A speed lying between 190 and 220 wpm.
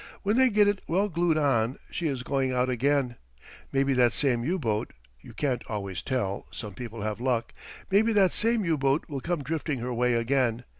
Yes: average, 200 wpm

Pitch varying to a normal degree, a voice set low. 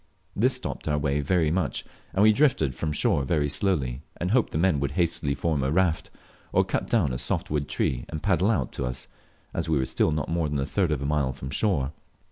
Yes: average, 4.5 semitones; very low, 75 Hz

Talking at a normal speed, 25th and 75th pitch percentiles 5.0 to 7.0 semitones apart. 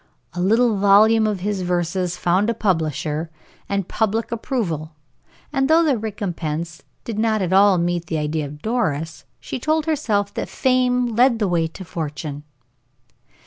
Yes: average, 160 wpm; wide, 5.4 semitones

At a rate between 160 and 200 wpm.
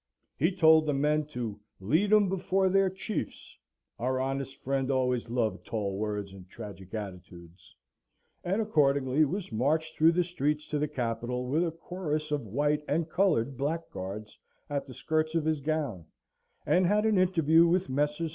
Yes: average, 165 wpm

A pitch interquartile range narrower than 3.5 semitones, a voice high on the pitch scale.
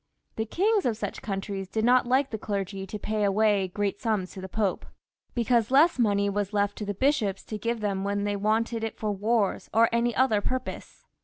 Yes: narrow, 2.6 semitones; high, 215 Hz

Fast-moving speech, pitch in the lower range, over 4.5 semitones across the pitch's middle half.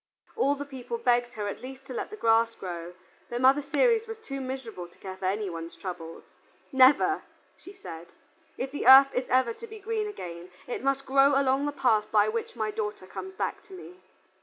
No: fast, 210 wpm; very high, 260 Hz; wide, 5.4 semitones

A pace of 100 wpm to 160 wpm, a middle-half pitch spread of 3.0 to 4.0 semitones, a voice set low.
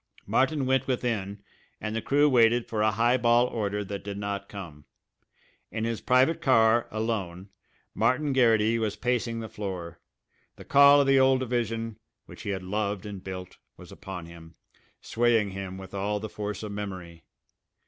No: average, 170 wpm; average, 3.4 semitones; low, 110 Hz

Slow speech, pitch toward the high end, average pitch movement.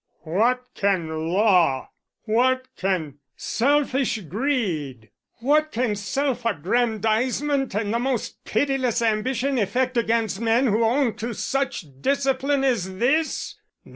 Yes: slow, 110 wpm; high, 235 Hz; average, 4.6 semitones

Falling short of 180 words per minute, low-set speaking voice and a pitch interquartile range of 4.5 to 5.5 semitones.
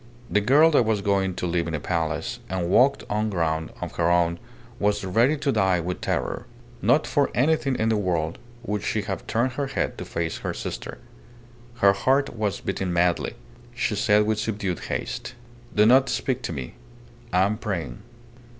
No: average, 185 wpm; low, 100 Hz; average, 5.1 semitones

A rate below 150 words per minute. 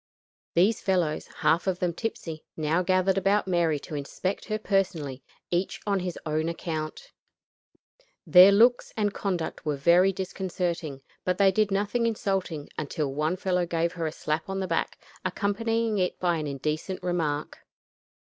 No: average, 155 wpm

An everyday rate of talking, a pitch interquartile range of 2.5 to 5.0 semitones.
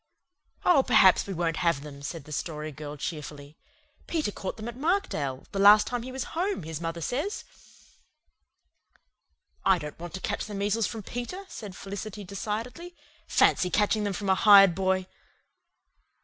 No: average, 165 wpm; wide, 5.6 semitones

